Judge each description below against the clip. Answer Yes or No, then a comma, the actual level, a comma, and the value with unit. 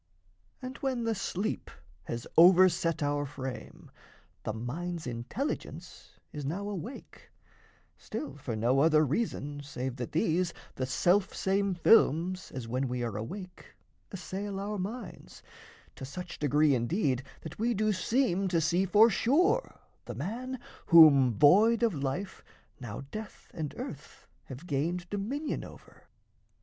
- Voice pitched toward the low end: No, medium, 175 Hz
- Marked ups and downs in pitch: Yes, wide, 6.9 semitones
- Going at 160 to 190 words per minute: No, slow, 135 wpm